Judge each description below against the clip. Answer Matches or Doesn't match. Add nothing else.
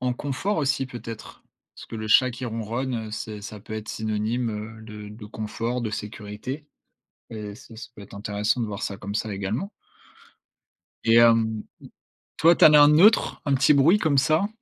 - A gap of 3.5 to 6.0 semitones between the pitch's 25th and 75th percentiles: Matches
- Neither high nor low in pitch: Doesn't match